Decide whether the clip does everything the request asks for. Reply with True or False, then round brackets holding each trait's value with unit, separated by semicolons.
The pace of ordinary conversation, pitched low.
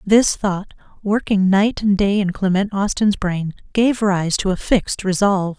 False (170 wpm; 195 Hz)